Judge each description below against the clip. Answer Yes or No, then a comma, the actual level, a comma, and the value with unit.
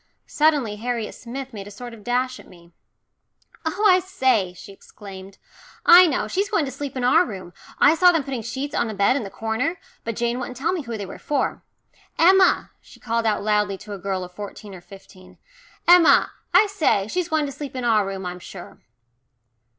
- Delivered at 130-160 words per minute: No, fast, 205 wpm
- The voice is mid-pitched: No, high, 240 Hz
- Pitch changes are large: Yes, wide, 6.8 semitones